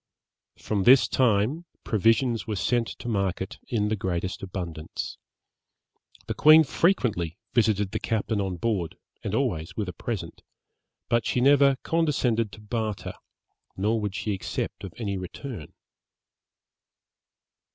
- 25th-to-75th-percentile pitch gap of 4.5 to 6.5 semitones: No, average, 4.0 semitones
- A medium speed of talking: No, slow, 130 wpm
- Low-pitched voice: Yes, low, 105 Hz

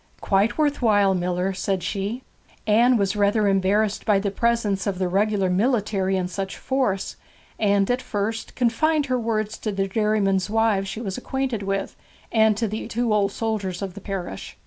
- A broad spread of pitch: No, narrow, 2.6 semitones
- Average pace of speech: Yes, average, 175 wpm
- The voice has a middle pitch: No, high, 205 Hz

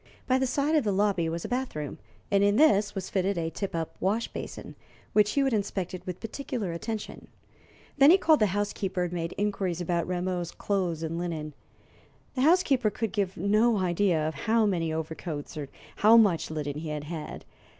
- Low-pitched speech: No, high, 195 Hz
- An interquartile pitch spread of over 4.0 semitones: Yes, average, 4.5 semitones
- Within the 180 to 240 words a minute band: Yes, average, 190 wpm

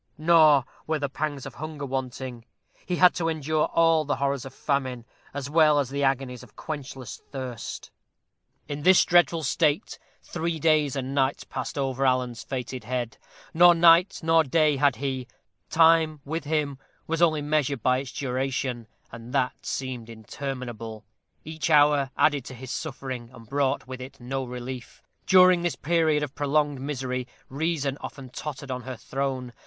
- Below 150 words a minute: No, average, 160 wpm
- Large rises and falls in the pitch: No, average, 3.2 semitones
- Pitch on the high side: No, medium, 140 Hz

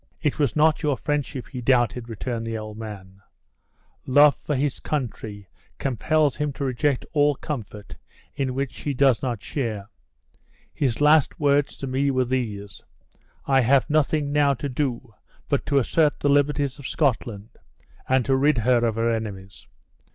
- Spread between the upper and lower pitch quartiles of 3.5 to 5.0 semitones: Yes, average, 4.0 semitones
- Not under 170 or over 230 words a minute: No, average, 160 wpm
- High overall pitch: No, low, 130 Hz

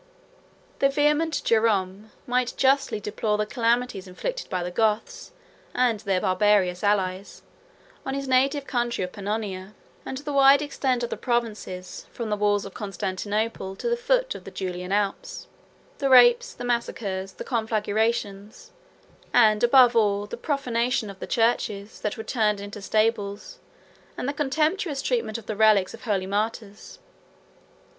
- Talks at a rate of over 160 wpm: No, average, 150 wpm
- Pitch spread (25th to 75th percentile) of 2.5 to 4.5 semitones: Yes, average, 4.2 semitones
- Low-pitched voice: No, high, 220 Hz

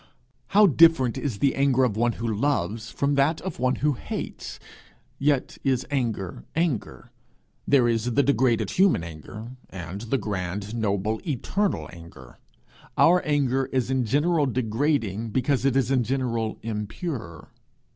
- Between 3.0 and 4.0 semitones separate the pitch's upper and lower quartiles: No, average, 4.6 semitones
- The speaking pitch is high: No, low, 125 Hz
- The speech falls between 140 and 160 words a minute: Yes, average, 145 wpm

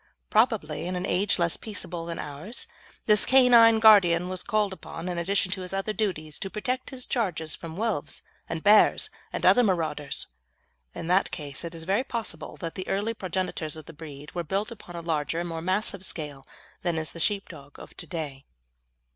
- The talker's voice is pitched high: No, medium, 180 Hz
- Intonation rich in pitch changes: No, average, 4.5 semitones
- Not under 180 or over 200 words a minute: Yes, average, 190 wpm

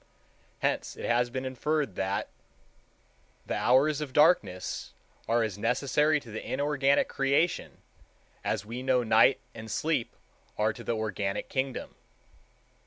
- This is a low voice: Yes, low, 125 Hz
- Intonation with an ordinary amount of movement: Yes, average, 4.3 semitones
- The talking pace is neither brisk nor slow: No, slow, 130 wpm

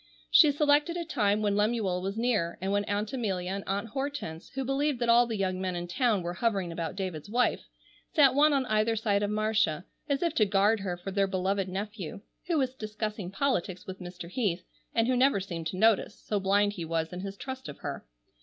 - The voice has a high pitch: Yes, high, 205 Hz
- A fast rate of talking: Yes, fast, 210 wpm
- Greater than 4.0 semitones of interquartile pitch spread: Yes, average, 4.4 semitones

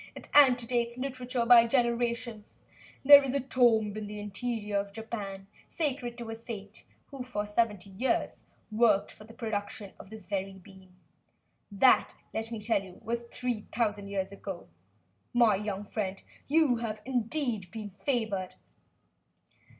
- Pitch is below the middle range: No, high, 225 Hz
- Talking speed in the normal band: Yes, average, 145 wpm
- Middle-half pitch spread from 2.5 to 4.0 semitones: Yes, average, 3.2 semitones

